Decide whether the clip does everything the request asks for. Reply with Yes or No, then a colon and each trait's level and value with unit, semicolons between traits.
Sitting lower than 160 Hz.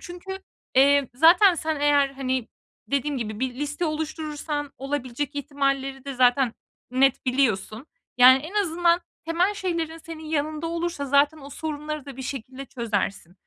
No: very high, 285 Hz